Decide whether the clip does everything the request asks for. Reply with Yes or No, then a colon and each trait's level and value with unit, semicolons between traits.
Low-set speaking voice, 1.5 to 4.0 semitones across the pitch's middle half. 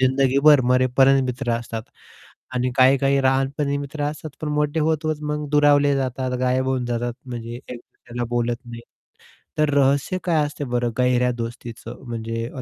Yes: low, 130 Hz; average, 2.9 semitones